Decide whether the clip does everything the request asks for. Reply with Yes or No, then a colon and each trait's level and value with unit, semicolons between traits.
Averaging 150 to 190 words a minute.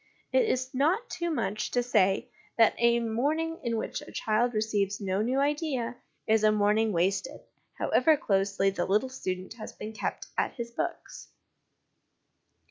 Yes: average, 155 wpm